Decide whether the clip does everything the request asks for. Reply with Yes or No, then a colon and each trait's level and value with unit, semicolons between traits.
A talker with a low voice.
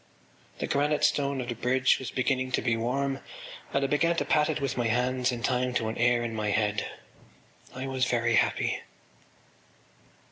Yes: low, 125 Hz